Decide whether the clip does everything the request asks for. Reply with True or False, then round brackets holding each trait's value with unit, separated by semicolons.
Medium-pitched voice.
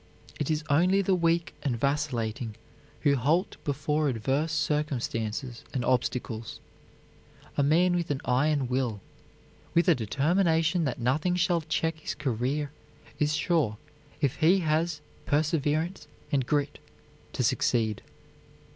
True (150 Hz)